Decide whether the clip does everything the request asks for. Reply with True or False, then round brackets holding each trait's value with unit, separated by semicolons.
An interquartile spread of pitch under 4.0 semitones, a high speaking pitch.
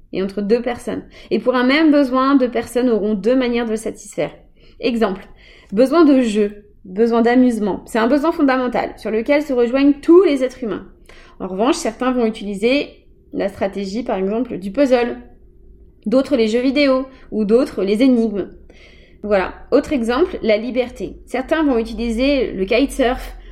True (3.3 semitones; 245 Hz)